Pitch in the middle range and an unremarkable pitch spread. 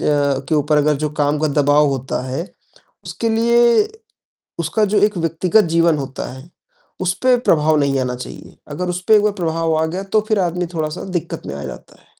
Yes: medium, 160 Hz; average, 3.7 semitones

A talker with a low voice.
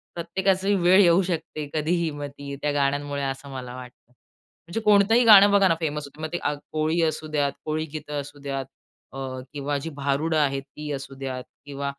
No: medium, 150 Hz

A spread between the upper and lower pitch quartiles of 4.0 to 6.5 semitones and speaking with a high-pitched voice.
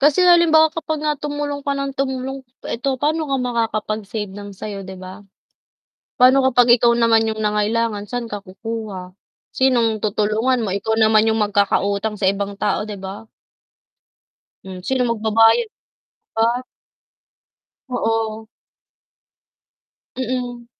No: average, 3.6 semitones; high, 225 Hz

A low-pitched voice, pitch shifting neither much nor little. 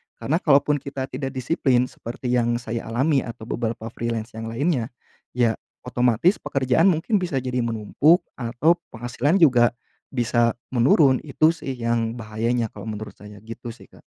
Yes: low, 120 Hz; average, 3.2 semitones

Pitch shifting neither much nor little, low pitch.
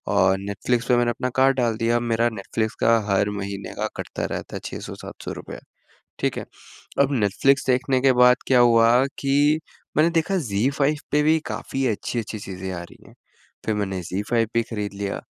Yes: average, 4.5 semitones; low, 120 Hz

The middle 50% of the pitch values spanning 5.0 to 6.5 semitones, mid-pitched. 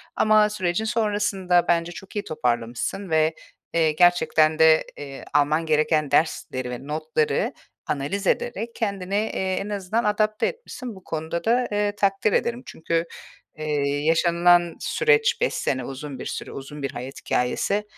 Yes: average, 5.3 semitones; medium, 175 Hz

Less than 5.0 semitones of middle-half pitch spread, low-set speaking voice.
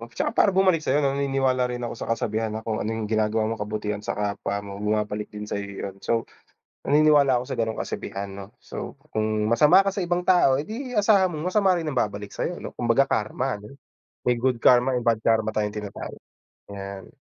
No: average, 5.3 semitones; low, 115 Hz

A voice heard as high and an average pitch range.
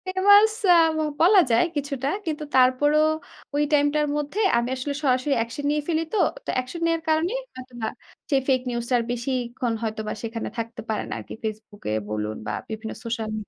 Yes: very high, 255 Hz; average, 4.6 semitones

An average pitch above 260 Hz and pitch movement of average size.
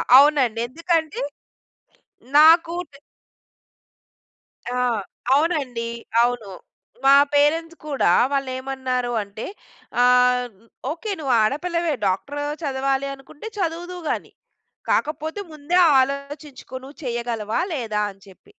Yes: very high, 275 Hz; average, 4.2 semitones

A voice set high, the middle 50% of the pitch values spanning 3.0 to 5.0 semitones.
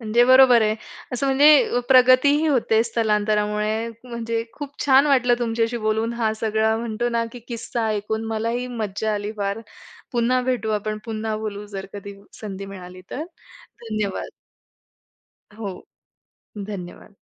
No: high, 225 Hz; narrow, 2.4 semitones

